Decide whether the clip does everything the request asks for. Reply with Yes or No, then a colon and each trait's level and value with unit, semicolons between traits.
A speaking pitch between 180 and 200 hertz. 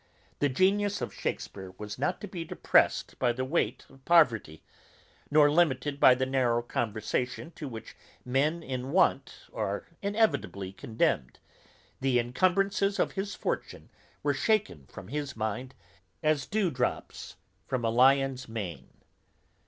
No: low, 135 Hz